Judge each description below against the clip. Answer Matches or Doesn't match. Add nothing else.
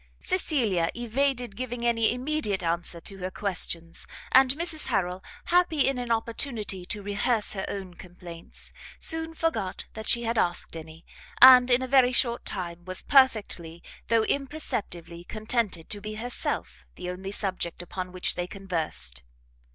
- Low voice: Doesn't match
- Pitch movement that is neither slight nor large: Doesn't match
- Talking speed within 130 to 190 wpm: Matches